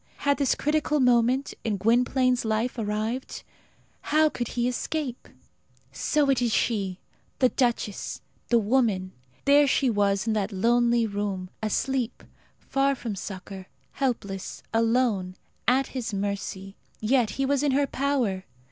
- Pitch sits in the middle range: No, high, 235 Hz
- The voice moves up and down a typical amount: Yes, average, 4.5 semitones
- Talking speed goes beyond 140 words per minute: No, slow, 135 wpm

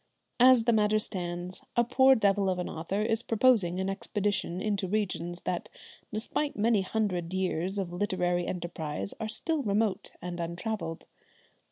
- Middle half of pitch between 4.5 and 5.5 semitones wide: No, average, 3.7 semitones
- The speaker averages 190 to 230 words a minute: No, average, 150 wpm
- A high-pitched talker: Yes, high, 195 Hz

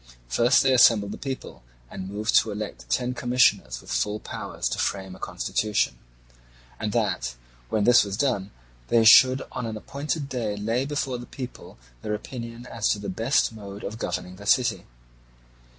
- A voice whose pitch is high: No, low, 110 Hz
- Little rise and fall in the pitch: No, average, 3.5 semitones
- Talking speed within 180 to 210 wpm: No, average, 170 wpm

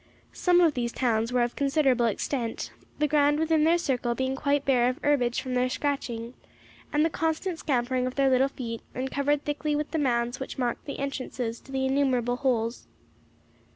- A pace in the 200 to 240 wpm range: No, average, 190 wpm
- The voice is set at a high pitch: Yes, very high, 265 Hz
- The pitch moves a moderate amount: Yes, average, 3.1 semitones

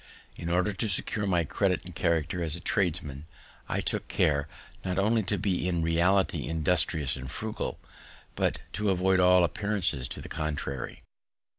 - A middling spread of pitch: Yes, average, 3.4 semitones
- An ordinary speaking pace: Yes, average, 160 wpm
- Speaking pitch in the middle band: No, very low, 90 Hz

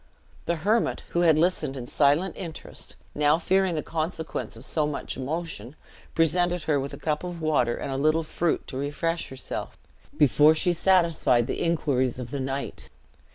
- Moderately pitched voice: Yes, medium, 155 Hz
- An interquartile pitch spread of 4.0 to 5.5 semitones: No, average, 3.5 semitones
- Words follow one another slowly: No, average, 170 wpm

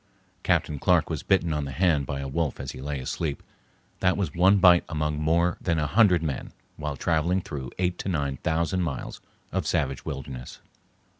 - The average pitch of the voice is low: Yes, very low, 80 Hz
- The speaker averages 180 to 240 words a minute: Yes, average, 190 wpm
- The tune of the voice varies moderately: Yes, average, 3.9 semitones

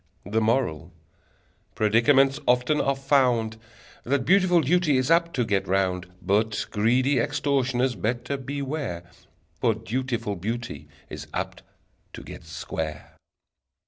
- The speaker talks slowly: Yes, slow, 115 wpm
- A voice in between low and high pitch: No, low, 125 Hz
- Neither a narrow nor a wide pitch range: Yes, average, 4.1 semitones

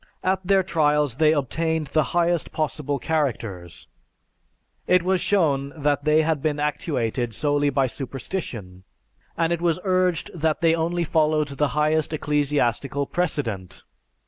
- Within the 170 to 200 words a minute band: No, slow, 135 wpm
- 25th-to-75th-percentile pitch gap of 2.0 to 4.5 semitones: Yes, average, 3.0 semitones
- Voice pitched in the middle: Yes, medium, 150 Hz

